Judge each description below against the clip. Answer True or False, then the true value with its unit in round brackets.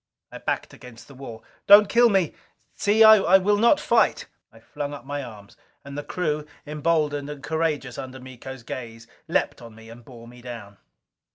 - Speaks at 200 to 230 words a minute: False (180 wpm)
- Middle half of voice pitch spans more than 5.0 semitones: True (5.6 semitones)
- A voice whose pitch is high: False (140 Hz)